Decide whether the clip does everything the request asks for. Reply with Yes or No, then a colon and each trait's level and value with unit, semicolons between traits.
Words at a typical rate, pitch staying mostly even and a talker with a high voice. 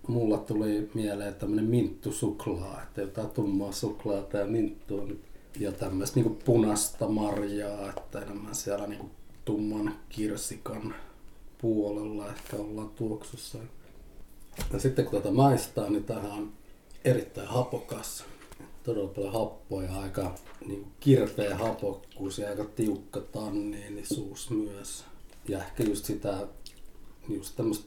No: average, 115 wpm; narrow, 1.4 semitones; low, 105 Hz